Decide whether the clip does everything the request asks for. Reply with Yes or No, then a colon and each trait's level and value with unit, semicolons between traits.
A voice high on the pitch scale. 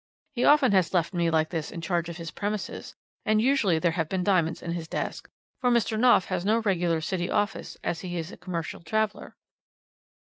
No: medium, 180 Hz